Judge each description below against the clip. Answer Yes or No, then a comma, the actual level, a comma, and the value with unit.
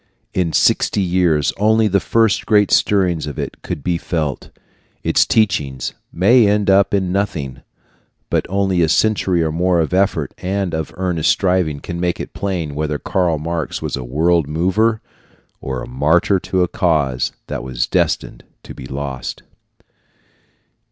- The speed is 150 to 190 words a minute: Yes, average, 155 wpm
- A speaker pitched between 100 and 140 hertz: No, very low, 85 Hz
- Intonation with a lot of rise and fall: No, average, 4.3 semitones